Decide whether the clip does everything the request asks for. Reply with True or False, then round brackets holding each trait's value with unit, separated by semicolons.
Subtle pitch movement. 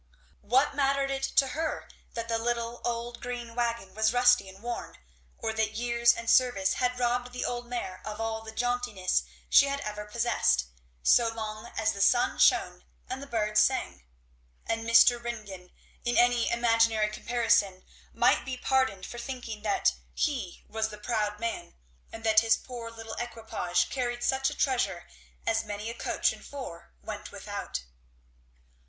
True (2.2 semitones)